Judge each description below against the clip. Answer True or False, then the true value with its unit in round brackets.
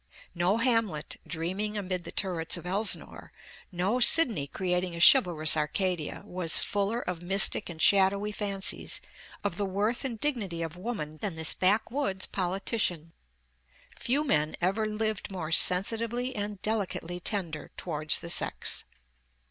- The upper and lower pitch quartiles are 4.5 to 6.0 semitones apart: False (3.8 semitones)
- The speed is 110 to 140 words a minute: True (135 wpm)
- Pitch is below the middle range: False (190 Hz)